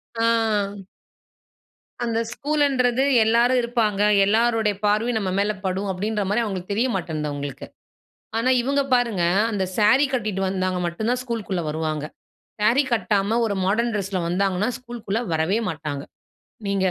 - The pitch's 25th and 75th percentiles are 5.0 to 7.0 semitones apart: No, average, 4.0 semitones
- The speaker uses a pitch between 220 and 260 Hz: No, high, 210 Hz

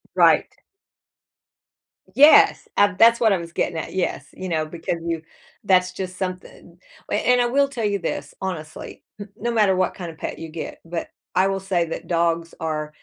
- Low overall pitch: No, medium, 185 Hz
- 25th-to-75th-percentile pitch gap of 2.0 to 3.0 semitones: No, average, 3.4 semitones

